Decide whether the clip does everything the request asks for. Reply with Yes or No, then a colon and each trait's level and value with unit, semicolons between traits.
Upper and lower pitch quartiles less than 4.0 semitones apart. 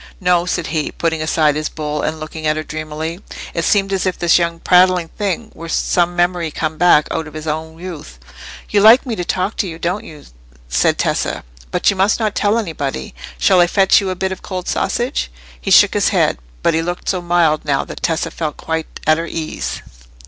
Yes: average, 2.8 semitones